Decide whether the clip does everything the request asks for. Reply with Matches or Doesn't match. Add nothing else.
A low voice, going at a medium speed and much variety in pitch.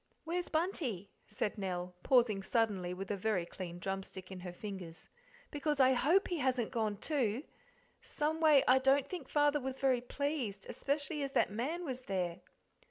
Doesn't match